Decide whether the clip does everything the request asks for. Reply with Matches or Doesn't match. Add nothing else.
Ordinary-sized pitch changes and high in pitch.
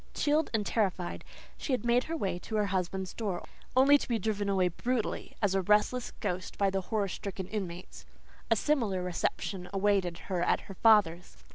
Matches